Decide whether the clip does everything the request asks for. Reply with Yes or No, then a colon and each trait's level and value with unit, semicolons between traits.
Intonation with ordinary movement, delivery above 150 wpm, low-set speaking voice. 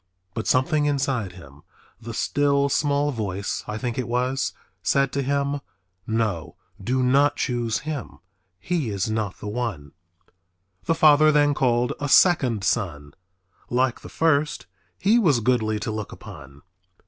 No: average, 4.7 semitones; average, 145 wpm; low, 125 Hz